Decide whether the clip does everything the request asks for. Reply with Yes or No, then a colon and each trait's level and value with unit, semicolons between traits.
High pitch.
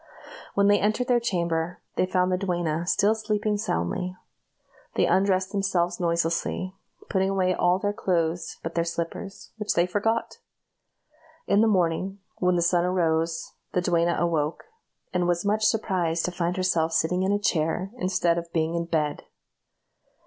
No: medium, 180 Hz